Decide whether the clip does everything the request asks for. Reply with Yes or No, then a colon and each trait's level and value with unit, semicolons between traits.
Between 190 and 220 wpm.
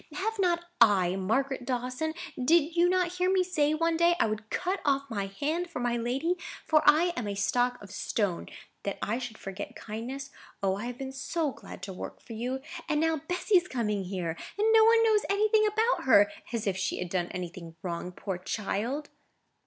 Yes: average, 200 wpm